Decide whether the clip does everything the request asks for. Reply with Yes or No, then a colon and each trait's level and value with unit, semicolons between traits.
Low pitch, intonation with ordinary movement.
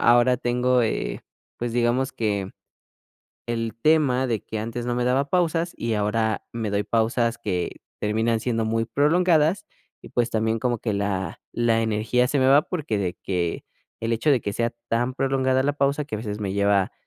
Yes: low, 115 Hz; average, 3.2 semitones